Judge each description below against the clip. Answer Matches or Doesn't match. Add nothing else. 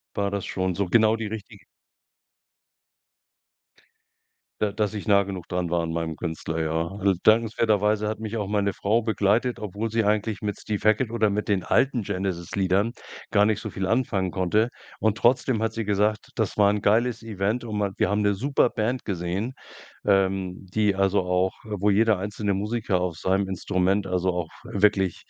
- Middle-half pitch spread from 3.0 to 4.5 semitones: Doesn't match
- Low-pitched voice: Matches